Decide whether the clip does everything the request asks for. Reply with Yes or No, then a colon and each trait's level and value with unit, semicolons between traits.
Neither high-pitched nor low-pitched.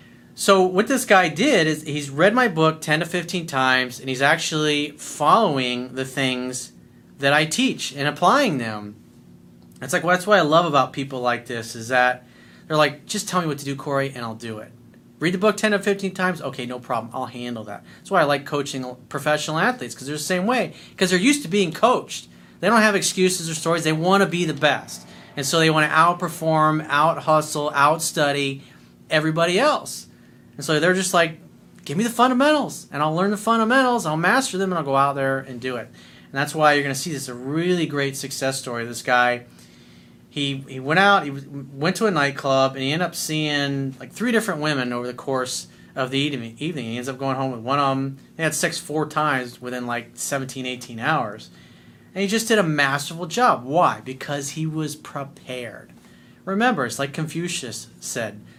Yes: medium, 145 Hz